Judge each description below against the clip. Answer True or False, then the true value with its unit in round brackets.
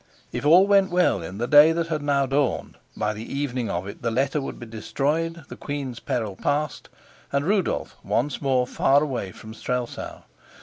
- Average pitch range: True (4.1 semitones)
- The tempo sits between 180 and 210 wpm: True (185 wpm)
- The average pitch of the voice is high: False (140 Hz)